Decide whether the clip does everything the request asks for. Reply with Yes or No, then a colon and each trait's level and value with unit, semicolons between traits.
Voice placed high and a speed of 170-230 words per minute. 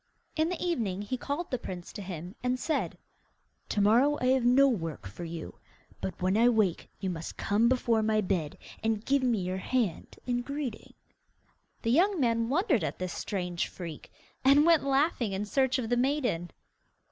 Yes: high, 230 Hz; average, 175 wpm